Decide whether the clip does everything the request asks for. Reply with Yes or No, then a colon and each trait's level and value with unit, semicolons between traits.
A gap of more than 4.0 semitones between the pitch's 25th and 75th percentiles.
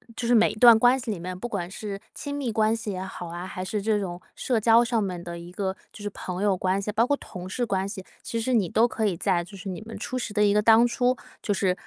No: average, 3.5 semitones